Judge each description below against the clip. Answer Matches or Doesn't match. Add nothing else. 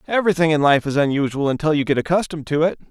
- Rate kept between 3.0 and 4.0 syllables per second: Doesn't match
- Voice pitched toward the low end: Doesn't match